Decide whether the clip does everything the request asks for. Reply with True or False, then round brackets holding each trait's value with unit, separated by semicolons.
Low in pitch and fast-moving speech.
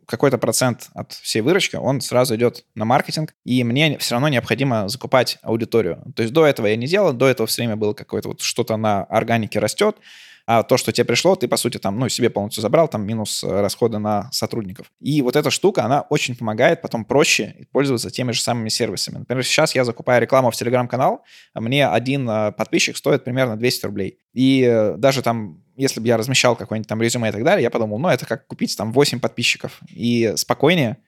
True (120 Hz; 205 wpm)